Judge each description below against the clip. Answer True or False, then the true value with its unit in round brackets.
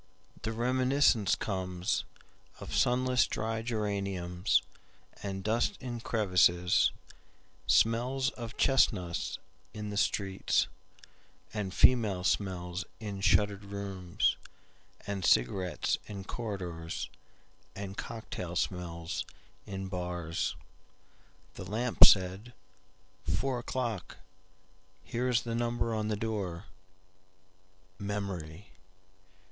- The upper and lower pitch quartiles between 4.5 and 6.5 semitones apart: False (3.3 semitones)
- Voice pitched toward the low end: True (95 Hz)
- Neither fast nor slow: False (70 wpm)